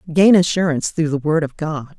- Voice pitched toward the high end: No, medium, 160 Hz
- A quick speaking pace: Yes, fast, 210 wpm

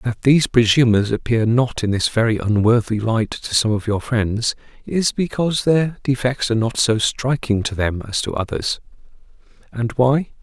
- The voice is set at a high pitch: No, low, 115 Hz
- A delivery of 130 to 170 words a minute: Yes, average, 165 wpm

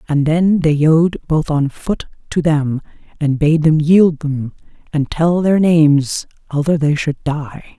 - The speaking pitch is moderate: Yes, medium, 155 Hz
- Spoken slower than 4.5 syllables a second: Yes, 3.8 syllables/s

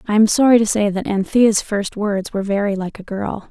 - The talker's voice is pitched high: Yes, high, 205 Hz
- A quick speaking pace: Yes, fast, 240 wpm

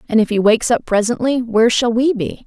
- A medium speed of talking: No, fast, 245 wpm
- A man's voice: No, female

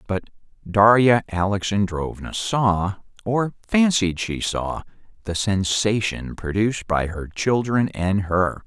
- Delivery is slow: Yes, slow, 110 wpm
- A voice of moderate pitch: No, low, 100 Hz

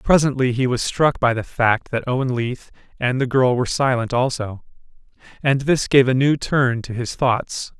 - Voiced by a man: Yes, male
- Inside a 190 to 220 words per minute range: Yes, average, 195 wpm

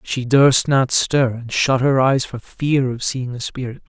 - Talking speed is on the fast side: Yes, fast, 215 wpm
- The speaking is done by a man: Yes, male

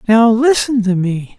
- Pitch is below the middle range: No, high, 220 Hz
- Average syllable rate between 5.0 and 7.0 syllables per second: No, 4.1 syllables/s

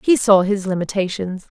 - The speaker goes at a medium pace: Yes, average, 150 wpm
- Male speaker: No, female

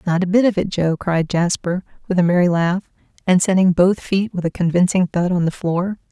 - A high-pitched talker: No, medium, 180 Hz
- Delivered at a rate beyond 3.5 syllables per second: Yes, 5.3 syllables/s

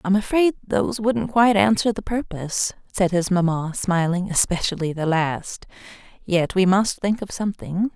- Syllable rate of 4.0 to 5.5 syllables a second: Yes, 4.9 syllables/s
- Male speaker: No, female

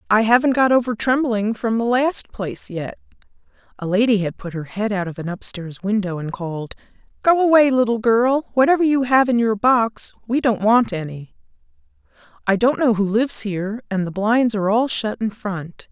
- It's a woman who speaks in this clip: Yes, female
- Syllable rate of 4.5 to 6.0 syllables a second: No, 3.5 syllables/s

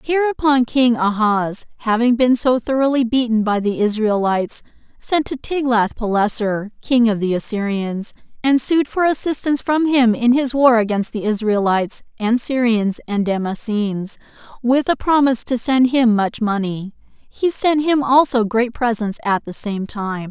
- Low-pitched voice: No, high, 235 Hz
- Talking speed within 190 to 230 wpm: No, average, 155 wpm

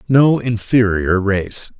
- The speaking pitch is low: Yes, low, 110 Hz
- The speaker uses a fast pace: No, slow, 100 wpm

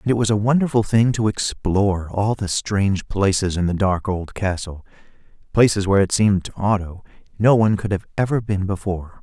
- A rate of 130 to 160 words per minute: No, average, 195 wpm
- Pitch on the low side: Yes, low, 100 Hz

